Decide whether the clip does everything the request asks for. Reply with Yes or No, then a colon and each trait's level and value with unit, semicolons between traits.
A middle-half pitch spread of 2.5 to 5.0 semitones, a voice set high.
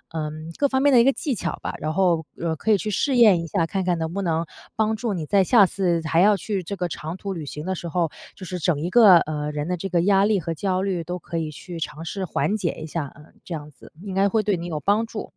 No: average, 3.7 semitones; medium, 180 Hz